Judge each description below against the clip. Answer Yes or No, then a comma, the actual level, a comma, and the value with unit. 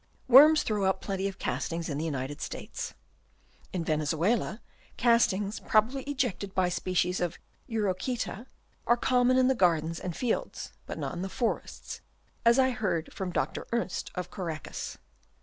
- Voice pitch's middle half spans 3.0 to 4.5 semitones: No, wide, 5.4 semitones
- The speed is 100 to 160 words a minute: Yes, average, 150 wpm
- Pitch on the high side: Yes, high, 195 Hz